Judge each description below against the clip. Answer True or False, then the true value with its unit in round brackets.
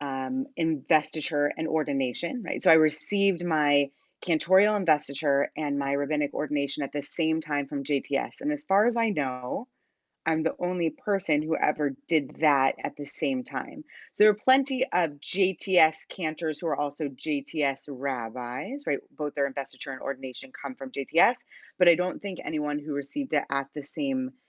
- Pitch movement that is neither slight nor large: True (4.1 semitones)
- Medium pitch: True (150 Hz)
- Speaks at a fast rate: False (175 wpm)